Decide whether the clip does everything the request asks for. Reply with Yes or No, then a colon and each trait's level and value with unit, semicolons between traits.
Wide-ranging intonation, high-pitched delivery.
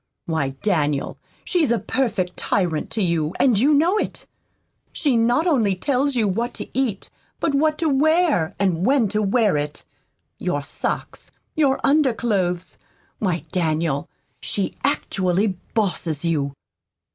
Yes: wide, 7.7 semitones; high, 210 Hz